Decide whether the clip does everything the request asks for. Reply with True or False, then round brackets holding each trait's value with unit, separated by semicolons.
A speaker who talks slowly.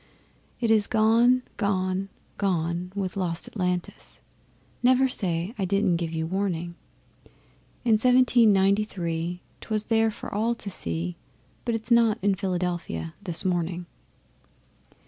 True (125 wpm)